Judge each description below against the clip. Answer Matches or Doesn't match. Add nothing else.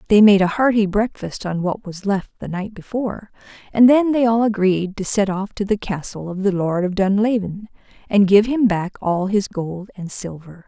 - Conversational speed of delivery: Doesn't match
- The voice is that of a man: Doesn't match